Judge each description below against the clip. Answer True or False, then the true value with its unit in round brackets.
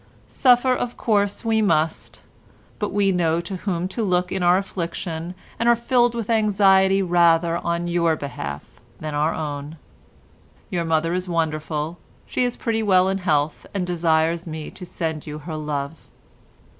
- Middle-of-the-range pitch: True (175 Hz)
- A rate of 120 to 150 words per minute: False (160 wpm)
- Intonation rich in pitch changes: False (3.7 semitones)